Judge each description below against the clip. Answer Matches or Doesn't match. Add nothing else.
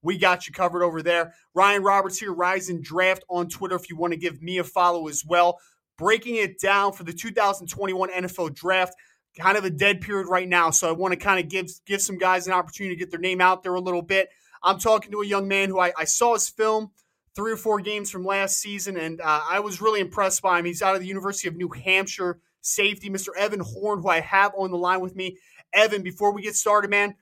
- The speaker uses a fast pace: Matches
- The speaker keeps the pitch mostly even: Matches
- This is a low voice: Doesn't match